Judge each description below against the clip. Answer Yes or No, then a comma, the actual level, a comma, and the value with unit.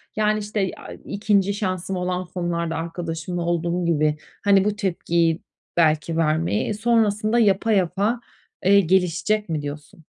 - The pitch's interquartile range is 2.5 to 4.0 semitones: Yes, average, 3.6 semitones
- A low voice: No, medium, 185 Hz